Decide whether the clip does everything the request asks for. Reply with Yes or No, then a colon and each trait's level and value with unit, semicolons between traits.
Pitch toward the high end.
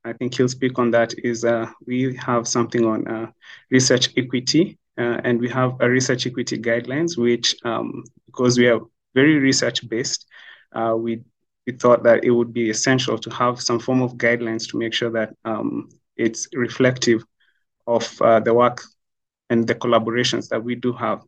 No: low, 120 Hz